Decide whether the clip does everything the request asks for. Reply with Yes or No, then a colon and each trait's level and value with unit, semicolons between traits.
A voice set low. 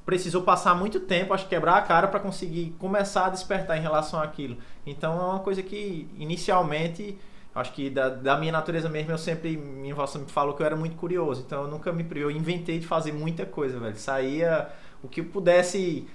No: medium, 165 Hz